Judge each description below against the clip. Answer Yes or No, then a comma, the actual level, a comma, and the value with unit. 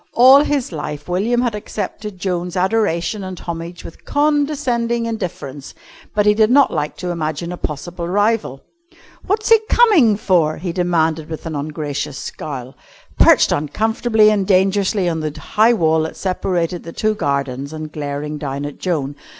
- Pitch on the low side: No, medium, 180 Hz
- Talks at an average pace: Yes, average, 160 wpm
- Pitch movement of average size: No, wide, 5.9 semitones